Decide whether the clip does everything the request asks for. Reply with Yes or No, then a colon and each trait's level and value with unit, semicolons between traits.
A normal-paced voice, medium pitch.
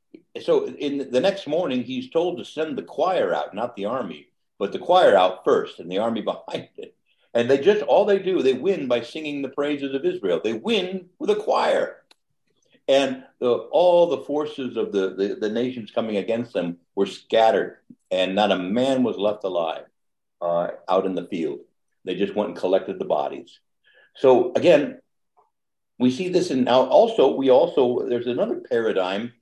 Yes: average, 185 wpm; medium, 150 Hz